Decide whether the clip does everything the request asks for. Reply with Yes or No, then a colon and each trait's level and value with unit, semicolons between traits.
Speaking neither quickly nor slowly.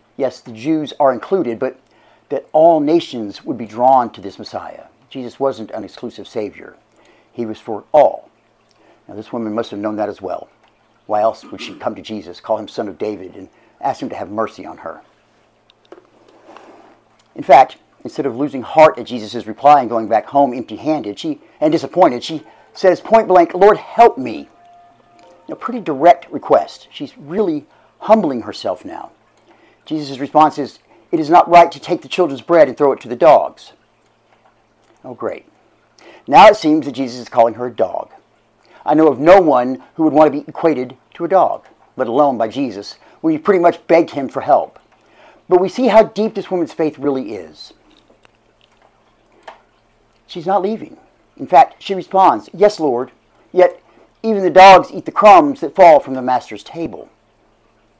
Yes: average, 180 wpm